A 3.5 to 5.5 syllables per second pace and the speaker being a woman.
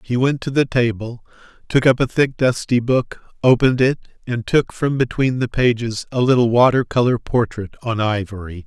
No: 5.0 syllables/s; male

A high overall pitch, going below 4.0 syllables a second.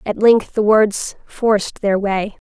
Yes: high, 205 Hz; 3.6 syllables/s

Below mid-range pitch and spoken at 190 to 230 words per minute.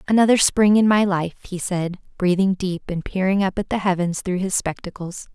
No: high, 190 Hz; average, 200 wpm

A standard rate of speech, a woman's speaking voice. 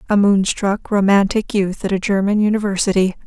Yes: average, 145 wpm; female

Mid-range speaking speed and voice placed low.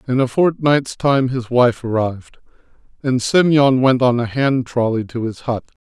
Yes: average, 175 wpm; low, 125 Hz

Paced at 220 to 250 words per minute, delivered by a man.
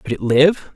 Yes: fast, 240 wpm; male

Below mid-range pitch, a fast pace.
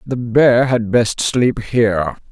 No: low, 115 Hz; average, 155 wpm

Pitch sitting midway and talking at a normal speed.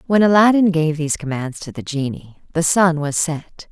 Yes: medium, 165 Hz; average, 195 wpm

